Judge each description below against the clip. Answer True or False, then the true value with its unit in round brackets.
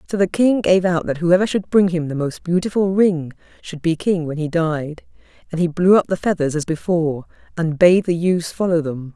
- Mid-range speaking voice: True (170 Hz)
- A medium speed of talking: False (225 wpm)